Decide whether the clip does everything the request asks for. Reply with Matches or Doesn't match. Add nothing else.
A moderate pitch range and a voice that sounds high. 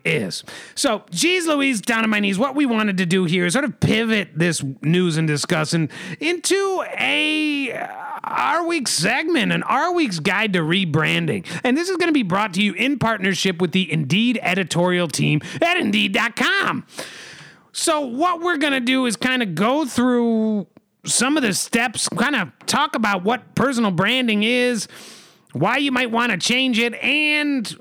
Doesn't match